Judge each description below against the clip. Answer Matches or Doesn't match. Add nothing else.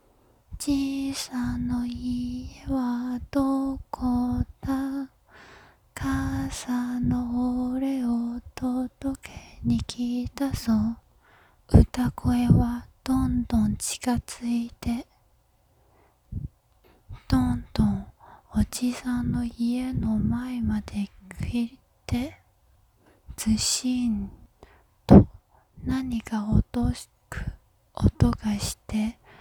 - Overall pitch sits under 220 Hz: Doesn't match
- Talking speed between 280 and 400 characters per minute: Doesn't match